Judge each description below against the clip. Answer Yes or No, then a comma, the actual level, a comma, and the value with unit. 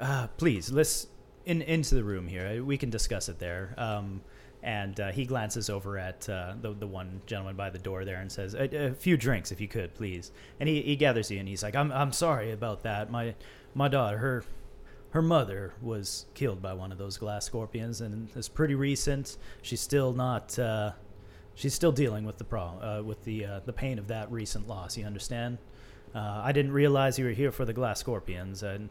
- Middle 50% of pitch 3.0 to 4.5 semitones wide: No, average, 4.9 semitones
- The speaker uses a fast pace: Yes, fast, 215 wpm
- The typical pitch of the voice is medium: No, low, 110 Hz